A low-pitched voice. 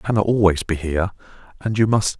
Yes: low, 100 Hz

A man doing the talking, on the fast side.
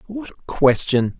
No: male; average, 150 wpm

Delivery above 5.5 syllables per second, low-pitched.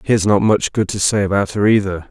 Yes: 6.0 syllables/s; low, 100 Hz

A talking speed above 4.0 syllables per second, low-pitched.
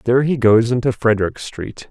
Yes: 5.7 syllables/s; low, 120 Hz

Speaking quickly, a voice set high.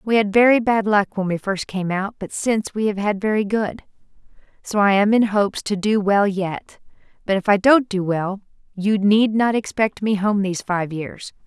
Yes: fast, 220 wpm; high, 205 Hz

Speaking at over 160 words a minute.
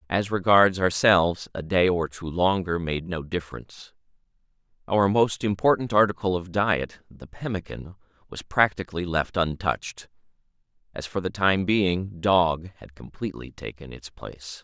No: average, 140 wpm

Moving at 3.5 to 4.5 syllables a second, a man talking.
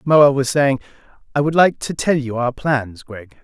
Yes: 4.4 syllables/s; male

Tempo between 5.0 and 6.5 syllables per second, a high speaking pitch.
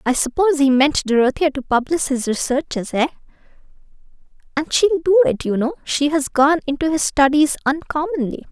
Yes: 5.5 syllables/s; very high, 290 Hz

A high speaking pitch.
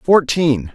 No: medium, 145 Hz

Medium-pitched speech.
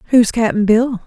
No: high, 225 Hz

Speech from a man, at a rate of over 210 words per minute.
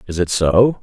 Yes: male; fast, 220 wpm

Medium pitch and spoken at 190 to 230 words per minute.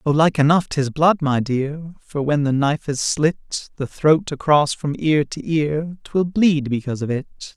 Yes: medium, 150 Hz; average, 200 wpm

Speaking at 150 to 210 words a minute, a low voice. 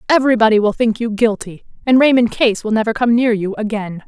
No: fast, 205 wpm; high, 225 Hz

